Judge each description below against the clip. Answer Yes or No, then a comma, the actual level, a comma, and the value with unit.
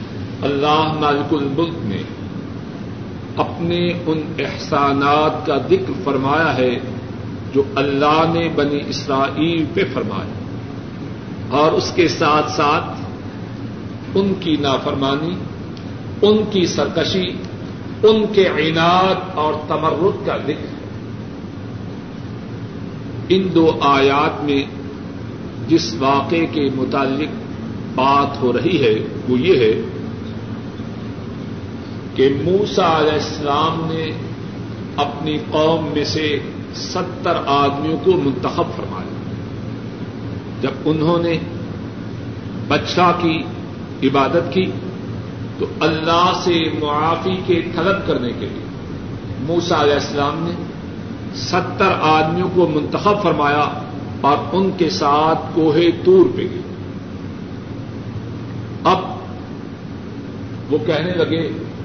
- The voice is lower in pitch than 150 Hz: Yes, medium, 140 Hz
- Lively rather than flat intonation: Yes, wide, 6.7 semitones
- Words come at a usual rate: No, slow, 100 wpm